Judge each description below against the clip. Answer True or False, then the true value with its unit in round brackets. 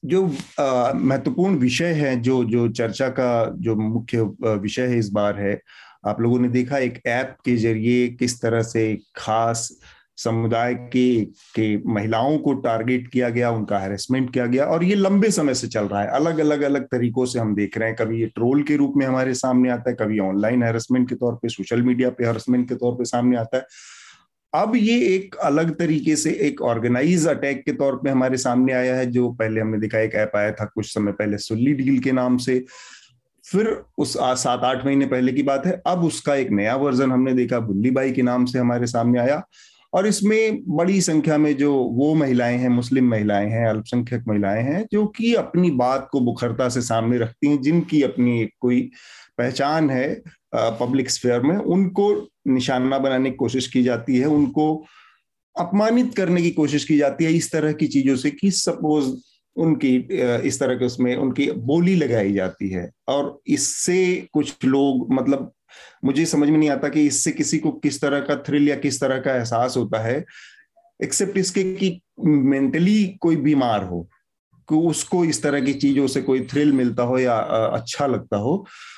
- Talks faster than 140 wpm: True (190 wpm)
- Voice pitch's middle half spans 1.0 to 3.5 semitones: False (3.9 semitones)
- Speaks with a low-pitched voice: True (130 Hz)